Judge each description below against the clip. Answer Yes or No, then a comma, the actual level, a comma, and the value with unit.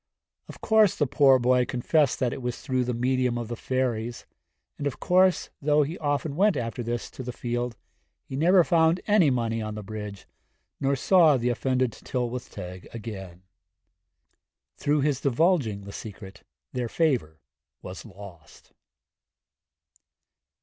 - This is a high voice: No, low, 125 Hz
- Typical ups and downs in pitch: Yes, average, 4.4 semitones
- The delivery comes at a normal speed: Yes, average, 150 wpm